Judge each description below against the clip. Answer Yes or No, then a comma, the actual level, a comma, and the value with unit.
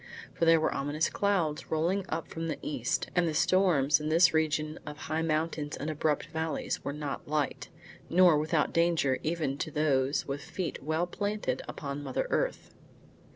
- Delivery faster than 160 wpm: Yes, average, 170 wpm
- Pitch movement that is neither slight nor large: No, narrow, 2.3 semitones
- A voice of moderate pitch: Yes, medium, 155 Hz